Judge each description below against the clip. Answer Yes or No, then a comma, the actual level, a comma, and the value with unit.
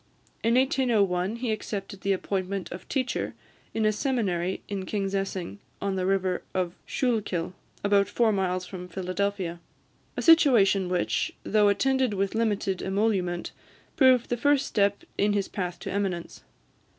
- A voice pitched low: No, high, 200 Hz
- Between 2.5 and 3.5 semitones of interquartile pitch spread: Yes, average, 3.0 semitones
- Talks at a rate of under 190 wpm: Yes, average, 140 wpm